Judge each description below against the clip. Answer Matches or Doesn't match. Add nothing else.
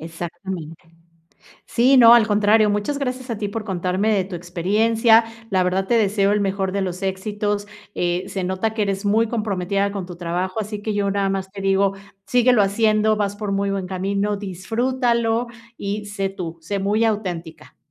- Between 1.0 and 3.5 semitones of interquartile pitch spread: Matches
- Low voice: Doesn't match